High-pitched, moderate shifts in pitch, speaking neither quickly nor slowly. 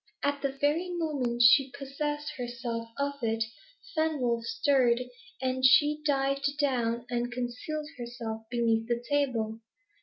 No: very high, 255 Hz; average, 3.2 semitones; slow, 125 wpm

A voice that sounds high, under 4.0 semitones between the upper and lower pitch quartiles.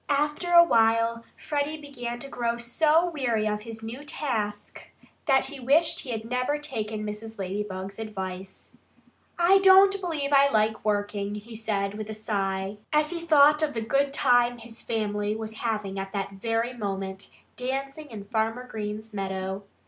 No: high, 225 Hz; average, 5.0 semitones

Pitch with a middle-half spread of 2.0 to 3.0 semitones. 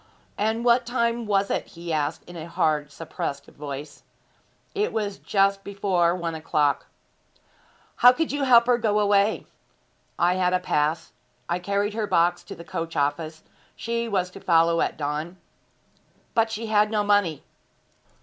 No: average, 4.8 semitones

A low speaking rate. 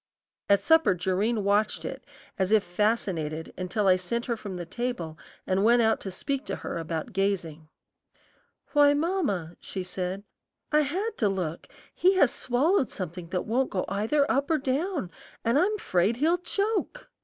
No: average, 165 wpm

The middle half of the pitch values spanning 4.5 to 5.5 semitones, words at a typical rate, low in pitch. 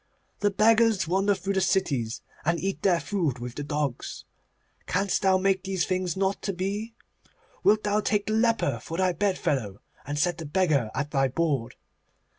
No: average, 5.2 semitones; average, 175 wpm; medium, 185 Hz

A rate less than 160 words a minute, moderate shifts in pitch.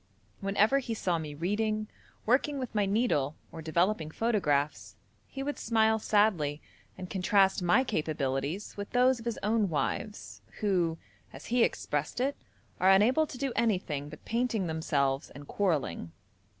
No: average, 150 wpm; wide, 6.3 semitones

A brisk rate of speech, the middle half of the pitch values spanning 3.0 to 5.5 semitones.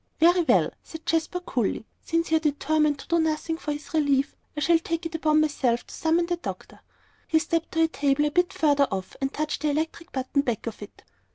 No: fast, 220 wpm; narrow, 2.6 semitones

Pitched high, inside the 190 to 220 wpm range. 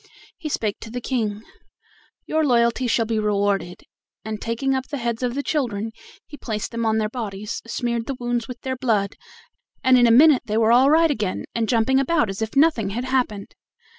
Yes: high, 235 Hz; average, 200 wpm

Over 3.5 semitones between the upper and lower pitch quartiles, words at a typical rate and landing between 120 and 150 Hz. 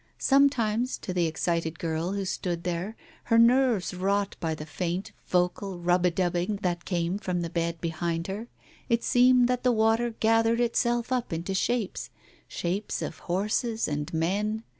No: average, 4.9 semitones; average, 165 wpm; high, 190 Hz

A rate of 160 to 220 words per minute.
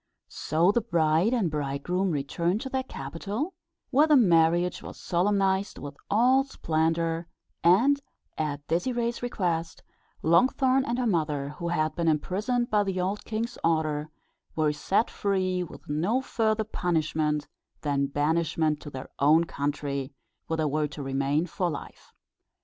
No: average, 145 wpm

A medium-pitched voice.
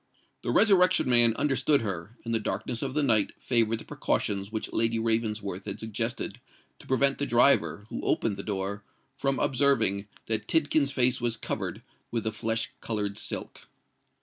No: low, 115 Hz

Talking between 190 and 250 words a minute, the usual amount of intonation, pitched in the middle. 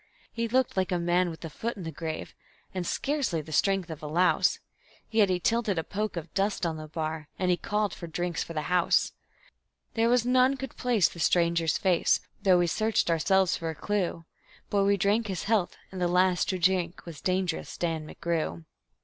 Yes: fast, 205 wpm; average, 3.5 semitones; medium, 180 Hz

